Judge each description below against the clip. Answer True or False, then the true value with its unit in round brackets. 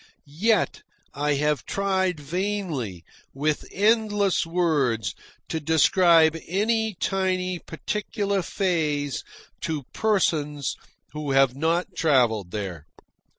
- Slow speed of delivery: True (95 wpm)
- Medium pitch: True (160 Hz)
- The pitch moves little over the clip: False (5.2 semitones)